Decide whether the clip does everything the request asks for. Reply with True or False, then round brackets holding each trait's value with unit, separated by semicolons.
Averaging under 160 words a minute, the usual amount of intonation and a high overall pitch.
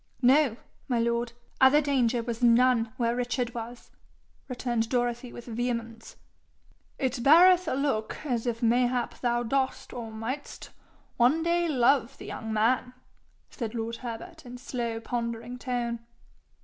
False (135 wpm; 2.0 semitones; 245 Hz)